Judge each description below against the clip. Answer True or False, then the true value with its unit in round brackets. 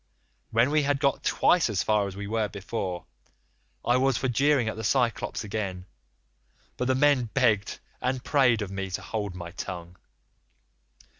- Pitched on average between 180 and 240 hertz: False (110 Hz)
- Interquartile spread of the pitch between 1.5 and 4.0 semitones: False (4.9 semitones)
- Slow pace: False (165 wpm)